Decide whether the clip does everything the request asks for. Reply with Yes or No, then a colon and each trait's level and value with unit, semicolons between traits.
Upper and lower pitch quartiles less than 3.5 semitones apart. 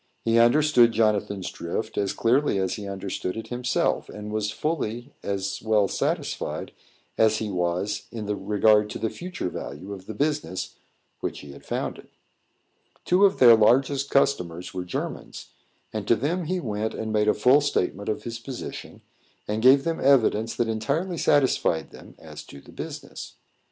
No: average, 4.8 semitones